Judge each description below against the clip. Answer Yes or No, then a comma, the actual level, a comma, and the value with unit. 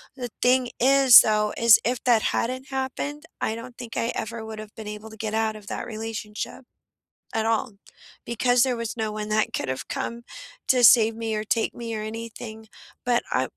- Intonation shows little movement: Yes, narrow, 2.0 semitones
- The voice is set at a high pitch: Yes, high, 225 Hz